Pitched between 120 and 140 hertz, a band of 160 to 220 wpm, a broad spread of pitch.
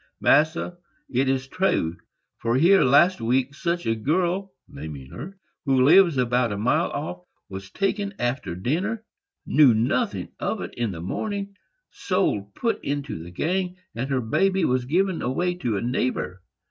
No: low, 135 Hz; average, 145 wpm; wide, 8.1 semitones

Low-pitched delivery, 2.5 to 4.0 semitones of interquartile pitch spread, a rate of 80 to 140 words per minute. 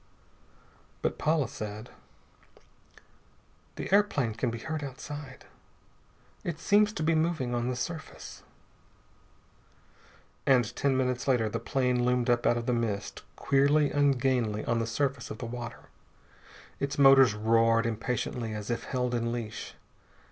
Yes: low, 125 Hz; average, 3.3 semitones; slow, 135 wpm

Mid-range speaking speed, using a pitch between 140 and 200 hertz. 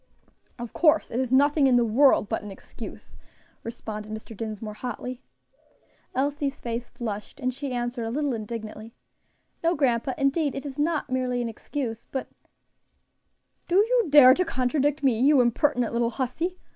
No: average, 160 wpm; very high, 255 Hz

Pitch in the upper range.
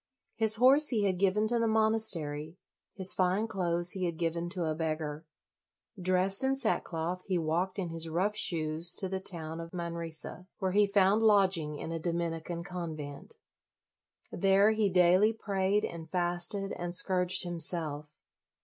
No: medium, 180 Hz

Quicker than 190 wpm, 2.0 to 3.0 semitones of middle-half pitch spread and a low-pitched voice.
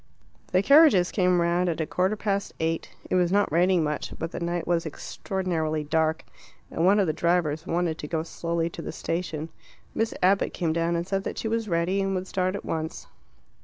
No: fast, 205 wpm; narrow, 2.6 semitones; medium, 175 Hz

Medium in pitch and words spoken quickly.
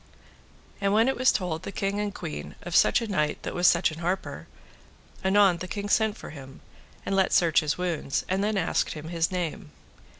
Yes: medium, 180 Hz; fast, 210 wpm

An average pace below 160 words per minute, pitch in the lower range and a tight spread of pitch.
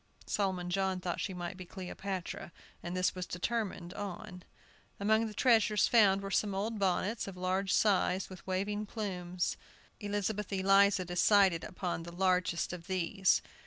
No: average, 150 wpm; high, 190 Hz; narrow, 2.2 semitones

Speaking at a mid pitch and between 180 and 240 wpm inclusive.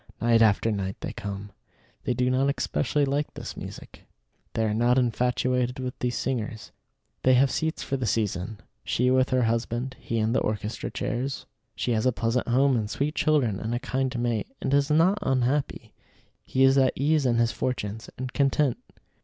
No: low, 125 Hz; average, 185 wpm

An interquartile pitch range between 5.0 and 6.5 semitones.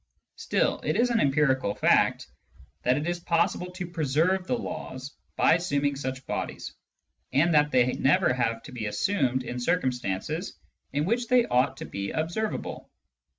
Yes: wide, 5.5 semitones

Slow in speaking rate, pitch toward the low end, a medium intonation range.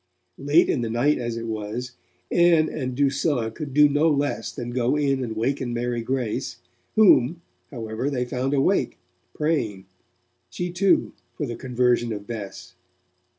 No: average, 150 wpm; low, 130 Hz; average, 3.7 semitones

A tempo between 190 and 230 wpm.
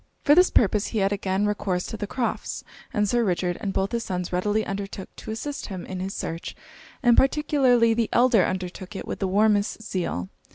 Yes: average, 200 wpm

